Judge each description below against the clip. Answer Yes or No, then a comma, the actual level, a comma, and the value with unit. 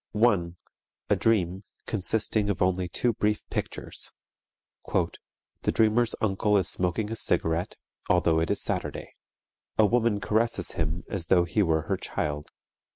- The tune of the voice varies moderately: Yes, average, 4.0 semitones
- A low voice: Yes, low, 100 Hz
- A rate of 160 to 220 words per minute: No, average, 140 wpm